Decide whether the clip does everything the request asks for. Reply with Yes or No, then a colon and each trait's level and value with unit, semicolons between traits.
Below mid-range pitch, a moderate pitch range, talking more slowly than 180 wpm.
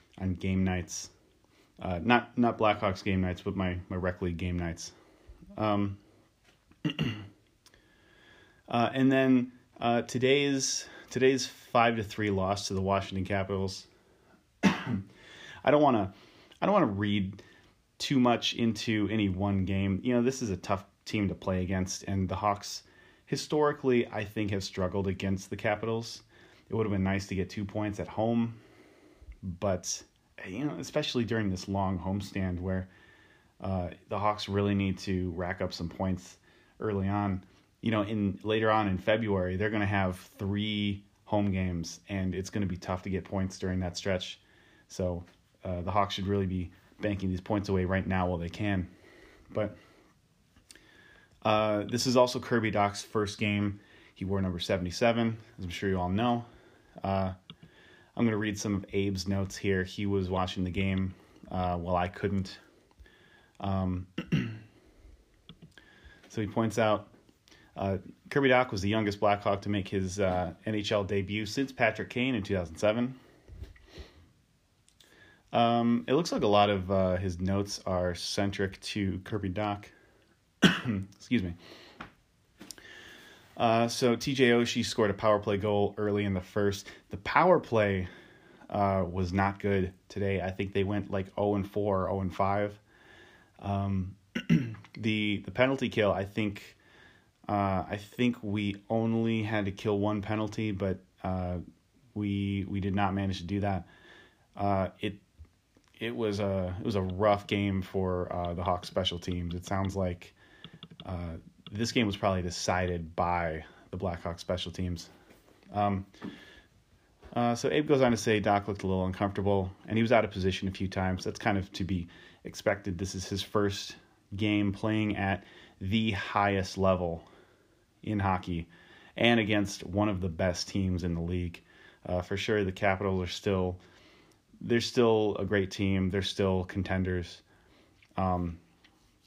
No: low, 100 Hz; narrow, 2.3 semitones; average, 160 wpm